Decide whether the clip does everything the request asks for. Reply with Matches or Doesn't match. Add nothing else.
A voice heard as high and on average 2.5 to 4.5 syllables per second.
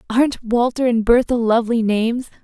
Doesn't match